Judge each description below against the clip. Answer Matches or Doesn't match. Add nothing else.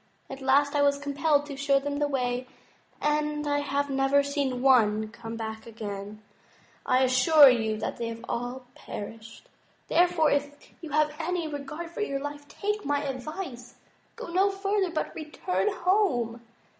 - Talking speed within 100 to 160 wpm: Matches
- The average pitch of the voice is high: Matches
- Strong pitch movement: Doesn't match